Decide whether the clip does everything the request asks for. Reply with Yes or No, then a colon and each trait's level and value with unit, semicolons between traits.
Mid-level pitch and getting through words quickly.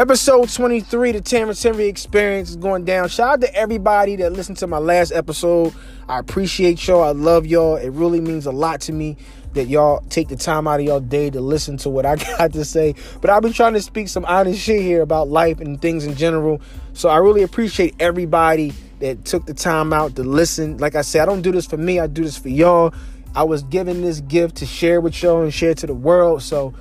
Yes: medium, 165 Hz; fast, 235 wpm